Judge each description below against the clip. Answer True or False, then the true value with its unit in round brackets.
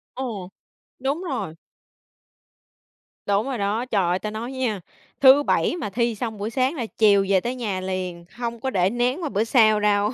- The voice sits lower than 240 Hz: True (220 Hz)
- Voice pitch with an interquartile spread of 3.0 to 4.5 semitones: True (4.1 semitones)